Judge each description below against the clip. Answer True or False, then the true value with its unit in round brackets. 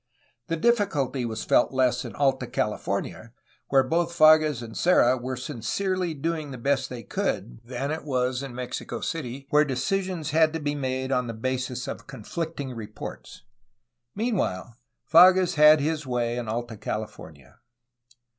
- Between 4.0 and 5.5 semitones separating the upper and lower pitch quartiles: True (4.5 semitones)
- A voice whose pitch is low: True (130 Hz)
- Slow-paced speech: False (145 wpm)